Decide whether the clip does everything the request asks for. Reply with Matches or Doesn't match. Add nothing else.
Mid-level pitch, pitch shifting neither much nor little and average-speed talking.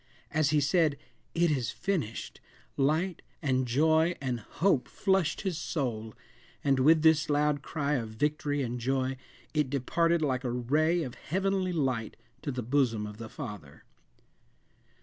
Matches